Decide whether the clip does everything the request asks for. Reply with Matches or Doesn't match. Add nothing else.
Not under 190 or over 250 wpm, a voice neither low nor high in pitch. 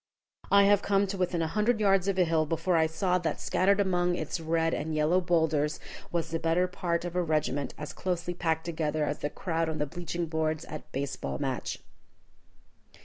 Matches